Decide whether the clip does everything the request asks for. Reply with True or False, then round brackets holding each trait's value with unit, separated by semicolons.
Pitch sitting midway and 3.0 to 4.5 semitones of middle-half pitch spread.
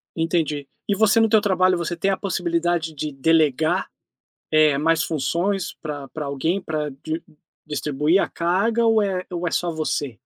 True (165 Hz; 3.4 semitones)